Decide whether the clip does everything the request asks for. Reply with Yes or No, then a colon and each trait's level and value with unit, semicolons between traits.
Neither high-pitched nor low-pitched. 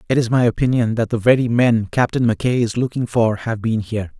No: low, 115 Hz